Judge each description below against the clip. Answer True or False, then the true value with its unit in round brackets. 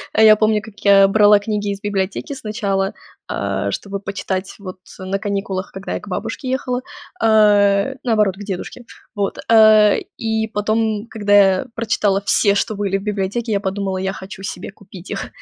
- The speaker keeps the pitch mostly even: True (1.9 semitones)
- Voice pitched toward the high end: True (205 Hz)